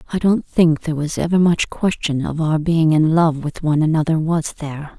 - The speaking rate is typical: No, fast, 215 wpm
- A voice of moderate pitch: Yes, medium, 160 Hz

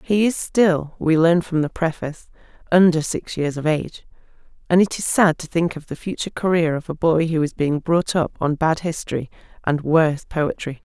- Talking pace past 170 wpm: Yes, fast, 205 wpm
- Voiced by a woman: Yes, female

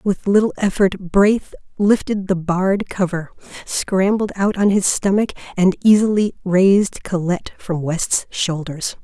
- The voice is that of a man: No, female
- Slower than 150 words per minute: Yes, slow, 135 wpm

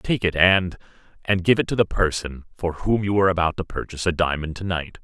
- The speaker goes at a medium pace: No, fast, 225 wpm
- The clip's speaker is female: No, male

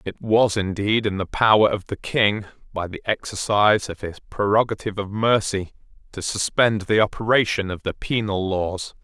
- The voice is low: Yes, low, 105 Hz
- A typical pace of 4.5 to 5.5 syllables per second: Yes, 4.9 syllables/s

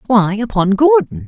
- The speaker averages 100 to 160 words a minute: Yes, average, 140 wpm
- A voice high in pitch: Yes, high, 215 Hz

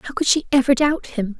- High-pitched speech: Yes, very high, 265 Hz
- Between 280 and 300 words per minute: No, fast, 260 wpm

